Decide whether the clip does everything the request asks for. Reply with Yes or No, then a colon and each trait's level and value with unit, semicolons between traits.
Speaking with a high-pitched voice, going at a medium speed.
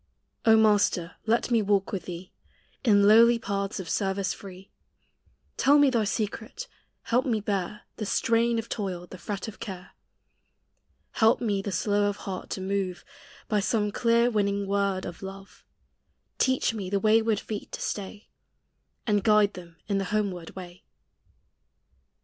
Yes: high, 205 Hz; average, 155 wpm